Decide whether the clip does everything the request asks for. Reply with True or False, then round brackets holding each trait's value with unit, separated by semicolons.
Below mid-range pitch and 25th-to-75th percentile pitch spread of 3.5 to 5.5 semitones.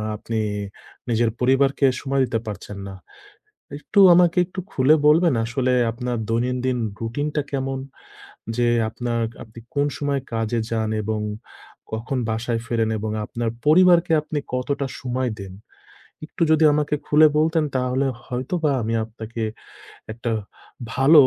True (125 Hz; 4.3 semitones)